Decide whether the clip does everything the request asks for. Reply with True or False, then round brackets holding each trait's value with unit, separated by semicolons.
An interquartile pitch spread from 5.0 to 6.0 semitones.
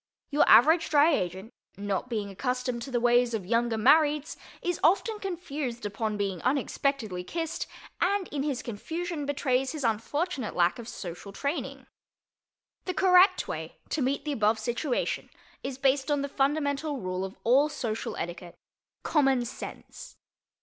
True (5.4 semitones)